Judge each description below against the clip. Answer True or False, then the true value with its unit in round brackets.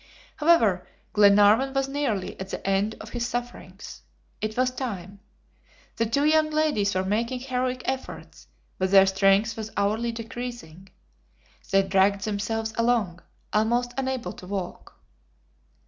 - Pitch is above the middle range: True (220 Hz)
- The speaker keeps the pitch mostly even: False (4.2 semitones)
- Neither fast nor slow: False (130 wpm)